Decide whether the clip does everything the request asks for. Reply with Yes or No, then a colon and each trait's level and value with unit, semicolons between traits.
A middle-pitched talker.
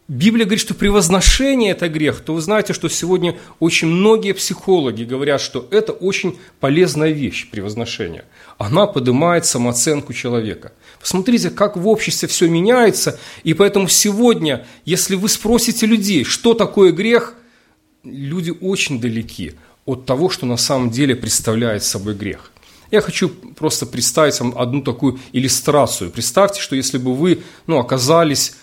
Yes: medium, 165 Hz